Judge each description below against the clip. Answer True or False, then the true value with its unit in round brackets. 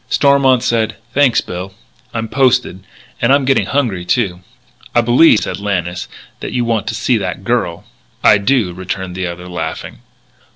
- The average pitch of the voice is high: False (110 Hz)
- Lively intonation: True (5.8 semitones)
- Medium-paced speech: True (160 wpm)